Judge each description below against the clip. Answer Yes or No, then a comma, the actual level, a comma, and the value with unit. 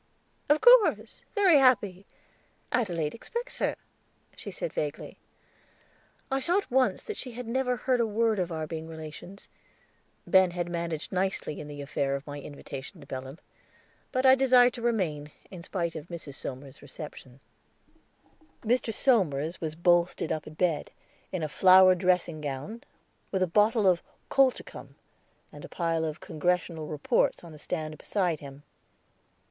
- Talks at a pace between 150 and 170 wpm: Yes, average, 155 wpm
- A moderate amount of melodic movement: No, wide, 7.1 semitones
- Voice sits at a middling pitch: Yes, medium, 175 Hz